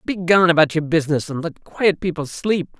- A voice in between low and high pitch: Yes, medium, 165 Hz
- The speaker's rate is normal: Yes, average, 195 wpm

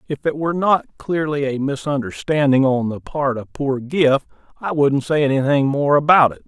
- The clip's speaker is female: No, male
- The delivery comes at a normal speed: Yes, average, 185 wpm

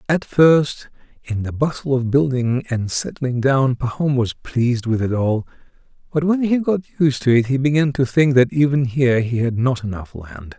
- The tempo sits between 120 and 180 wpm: No, average, 200 wpm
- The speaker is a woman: No, male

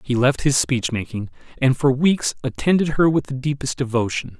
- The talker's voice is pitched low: Yes, low, 130 Hz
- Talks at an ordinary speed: Yes, average, 190 wpm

